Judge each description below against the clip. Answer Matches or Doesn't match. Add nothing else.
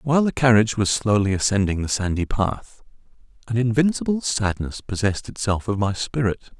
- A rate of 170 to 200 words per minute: Doesn't match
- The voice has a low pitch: Matches